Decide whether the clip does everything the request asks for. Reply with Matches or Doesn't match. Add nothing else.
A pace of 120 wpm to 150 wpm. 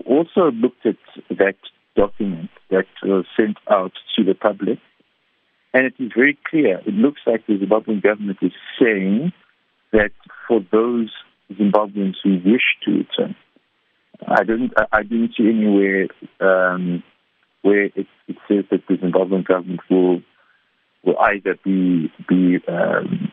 Matches